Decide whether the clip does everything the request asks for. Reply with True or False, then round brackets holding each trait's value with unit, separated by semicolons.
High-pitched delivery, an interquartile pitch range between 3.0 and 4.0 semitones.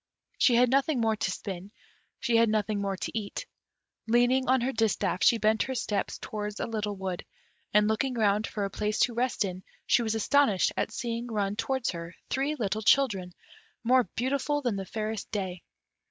True (220 Hz; 3.3 semitones)